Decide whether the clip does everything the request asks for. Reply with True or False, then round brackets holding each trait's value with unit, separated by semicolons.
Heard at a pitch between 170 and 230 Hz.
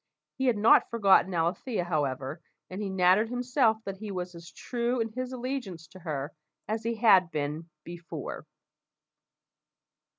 True (190 Hz)